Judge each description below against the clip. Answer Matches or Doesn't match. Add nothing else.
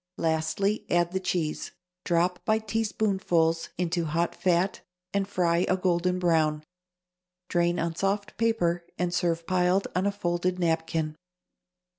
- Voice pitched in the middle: Matches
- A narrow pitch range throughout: Matches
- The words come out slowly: Matches